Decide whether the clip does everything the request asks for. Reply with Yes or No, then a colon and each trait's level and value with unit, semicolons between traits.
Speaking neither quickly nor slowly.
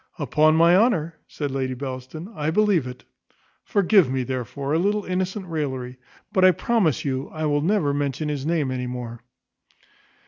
Yes: average, 165 wpm